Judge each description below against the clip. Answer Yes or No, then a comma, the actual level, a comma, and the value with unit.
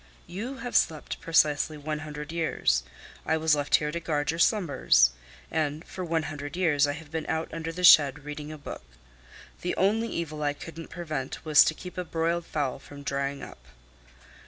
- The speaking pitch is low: No, medium, 155 Hz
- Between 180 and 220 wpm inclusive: Yes, average, 185 wpm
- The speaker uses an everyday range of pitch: No, narrow, 2.3 semitones